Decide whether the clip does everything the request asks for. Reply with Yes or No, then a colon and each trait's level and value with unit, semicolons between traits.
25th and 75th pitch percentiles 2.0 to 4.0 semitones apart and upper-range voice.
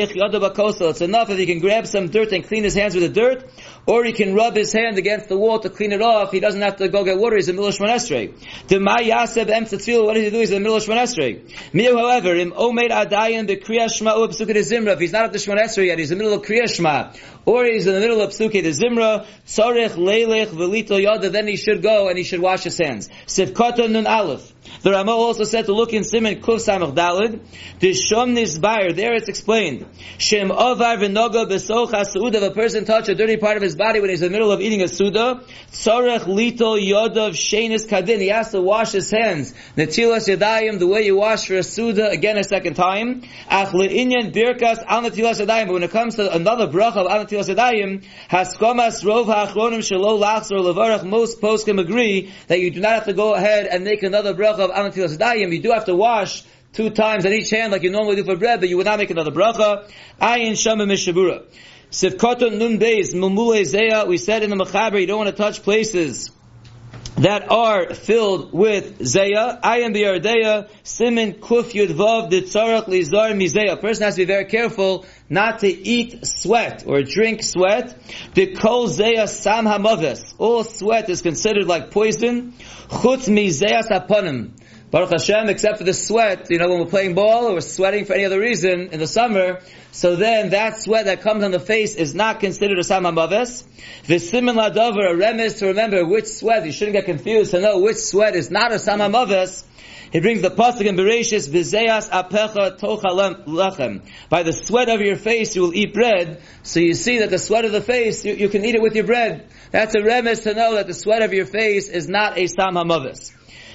Yes: average, 2.8 semitones; high, 210 Hz